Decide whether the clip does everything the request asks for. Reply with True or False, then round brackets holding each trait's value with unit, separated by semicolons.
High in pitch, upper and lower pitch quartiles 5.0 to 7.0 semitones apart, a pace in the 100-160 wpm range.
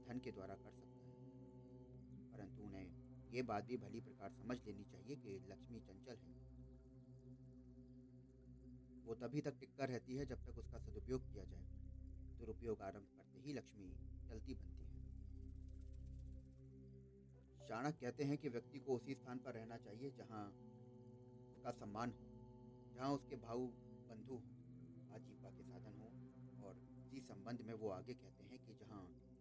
False (120 Hz; 5.4 semitones; 150 wpm)